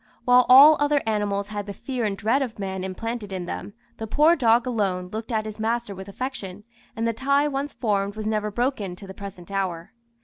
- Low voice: No, high, 215 Hz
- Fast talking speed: Yes, fast, 210 wpm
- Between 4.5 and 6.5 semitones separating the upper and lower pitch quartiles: No, average, 3.9 semitones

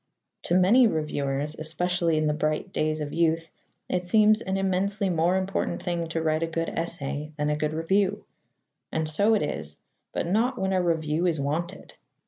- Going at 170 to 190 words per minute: Yes, average, 180 wpm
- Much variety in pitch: No, average, 3.5 semitones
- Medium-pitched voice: Yes, medium, 165 Hz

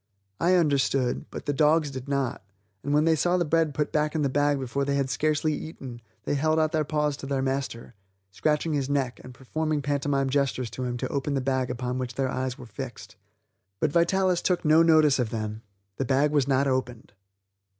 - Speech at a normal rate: No, fast, 210 wpm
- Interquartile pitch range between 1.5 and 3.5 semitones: Yes, average, 2.8 semitones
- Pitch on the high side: No, medium, 140 Hz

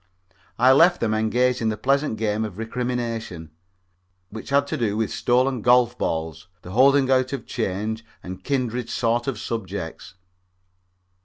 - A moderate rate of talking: Yes, average, 145 wpm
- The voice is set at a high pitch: No, low, 115 Hz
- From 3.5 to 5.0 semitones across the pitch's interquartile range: No, average, 2.9 semitones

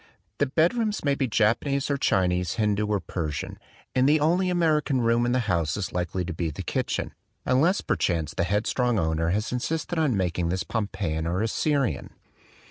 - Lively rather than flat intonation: Yes, wide, 8.0 semitones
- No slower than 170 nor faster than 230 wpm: Yes, average, 185 wpm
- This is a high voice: No, low, 110 Hz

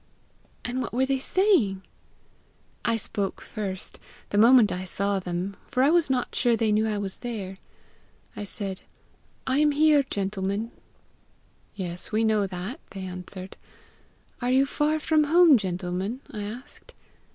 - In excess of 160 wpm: No, average, 150 wpm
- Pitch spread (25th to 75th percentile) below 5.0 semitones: No, average, 5.3 semitones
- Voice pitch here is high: Yes, high, 215 Hz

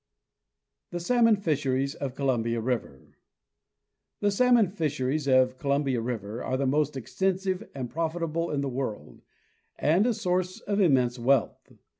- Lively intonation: Yes, wide, 5.9 semitones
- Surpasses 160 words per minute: No, slow, 135 wpm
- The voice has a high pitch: No, medium, 140 Hz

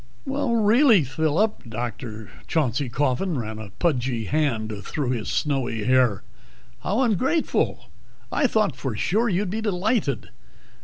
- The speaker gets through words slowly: Yes, slow, 120 wpm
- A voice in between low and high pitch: Yes, medium, 145 Hz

